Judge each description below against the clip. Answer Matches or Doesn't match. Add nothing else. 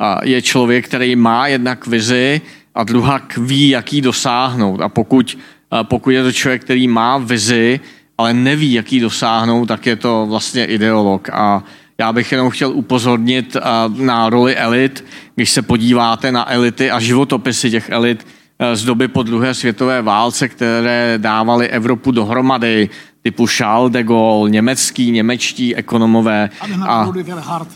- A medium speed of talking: Matches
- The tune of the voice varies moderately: Doesn't match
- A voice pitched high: Doesn't match